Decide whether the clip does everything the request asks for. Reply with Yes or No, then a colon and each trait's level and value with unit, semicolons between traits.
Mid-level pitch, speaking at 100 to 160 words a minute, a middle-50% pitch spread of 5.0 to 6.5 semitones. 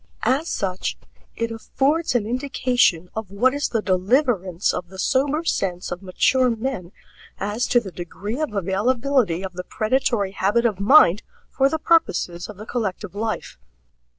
No: high, 220 Hz; average, 155 wpm; wide, 5.4 semitones